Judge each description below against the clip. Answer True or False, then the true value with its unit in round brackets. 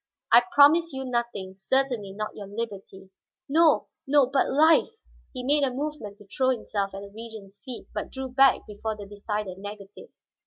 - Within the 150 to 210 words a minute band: True (170 wpm)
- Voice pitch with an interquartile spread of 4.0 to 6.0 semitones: True (5.0 semitones)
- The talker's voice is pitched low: False (230 Hz)